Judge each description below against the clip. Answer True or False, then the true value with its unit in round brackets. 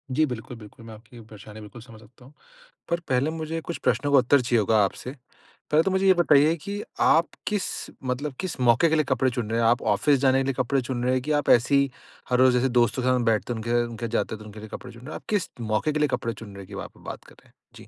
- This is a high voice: False (125 Hz)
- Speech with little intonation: False (4.3 semitones)